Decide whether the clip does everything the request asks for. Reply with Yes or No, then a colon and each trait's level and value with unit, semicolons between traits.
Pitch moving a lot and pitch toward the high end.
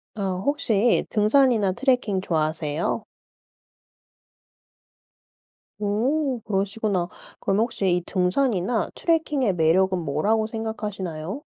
No: average, 4.7 semitones; high, 210 Hz